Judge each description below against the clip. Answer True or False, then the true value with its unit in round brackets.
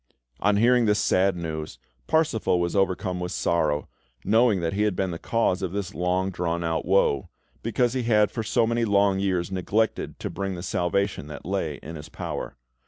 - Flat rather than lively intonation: False (3.5 semitones)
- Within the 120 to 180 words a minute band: False (190 wpm)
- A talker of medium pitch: False (95 Hz)